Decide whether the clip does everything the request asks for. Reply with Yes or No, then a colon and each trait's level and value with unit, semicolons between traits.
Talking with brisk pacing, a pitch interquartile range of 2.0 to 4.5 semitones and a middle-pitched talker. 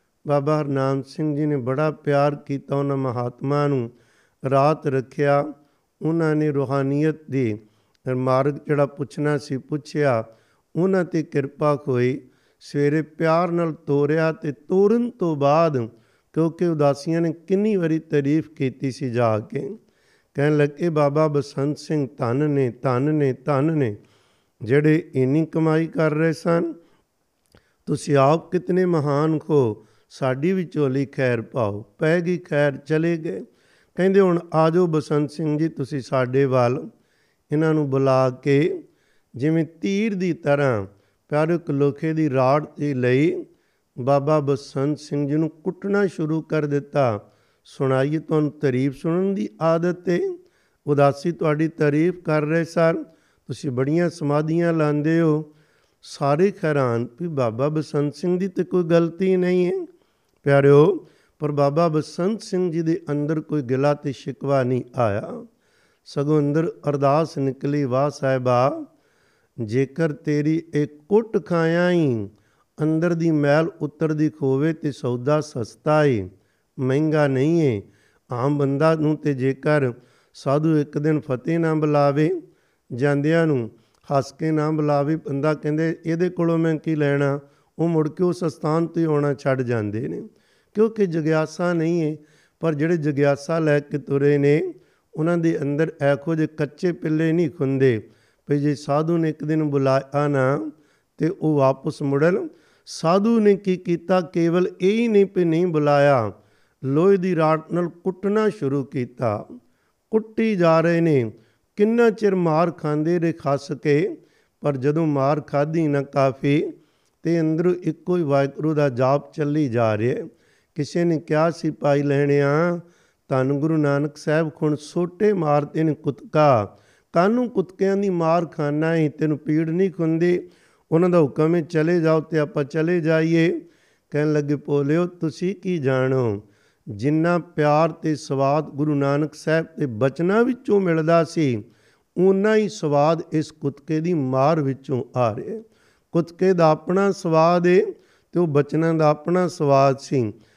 No: average, 145 wpm; average, 3.0 semitones; medium, 150 Hz